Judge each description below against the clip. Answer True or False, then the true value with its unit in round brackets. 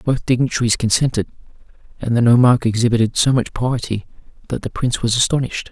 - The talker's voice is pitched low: True (120 Hz)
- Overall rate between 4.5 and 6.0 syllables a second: False (6.5 syllables/s)